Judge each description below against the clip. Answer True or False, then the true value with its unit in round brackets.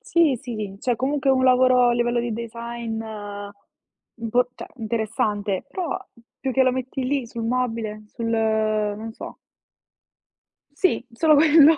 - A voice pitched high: True (240 Hz)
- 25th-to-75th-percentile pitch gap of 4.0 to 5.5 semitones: False (2.7 semitones)